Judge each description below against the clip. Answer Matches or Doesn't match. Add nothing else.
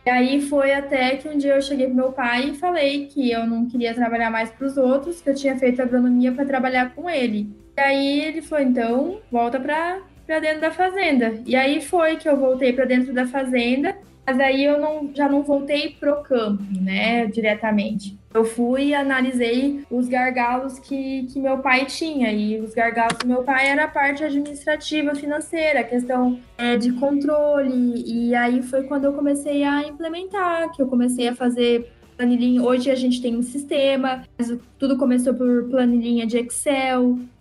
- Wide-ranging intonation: Doesn't match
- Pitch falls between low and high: Doesn't match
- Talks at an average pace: Doesn't match